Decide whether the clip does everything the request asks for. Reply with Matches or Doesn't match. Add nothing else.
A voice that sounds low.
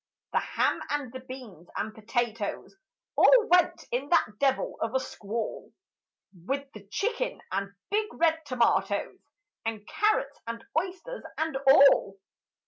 Doesn't match